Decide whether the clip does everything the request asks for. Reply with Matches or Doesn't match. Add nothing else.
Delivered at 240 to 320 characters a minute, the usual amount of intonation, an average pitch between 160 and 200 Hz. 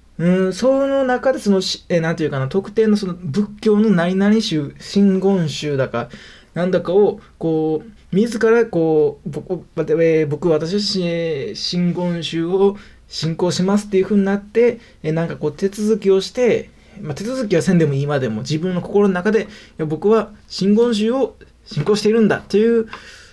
Matches